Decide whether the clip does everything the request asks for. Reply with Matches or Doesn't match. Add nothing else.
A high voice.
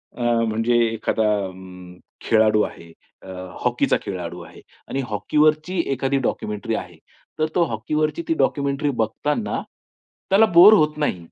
Doesn't match